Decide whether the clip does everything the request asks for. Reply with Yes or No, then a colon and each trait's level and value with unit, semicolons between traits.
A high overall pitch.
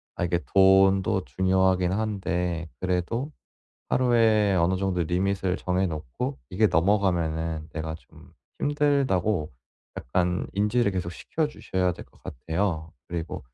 No: very low, 95 Hz